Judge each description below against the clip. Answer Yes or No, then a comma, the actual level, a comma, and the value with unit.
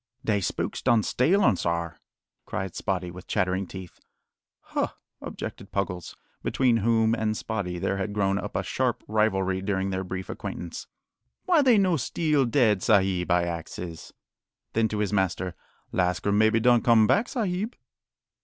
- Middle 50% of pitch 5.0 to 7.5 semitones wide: No, average, 3.8 semitones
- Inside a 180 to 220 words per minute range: No, average, 155 wpm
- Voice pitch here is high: No, low, 100 Hz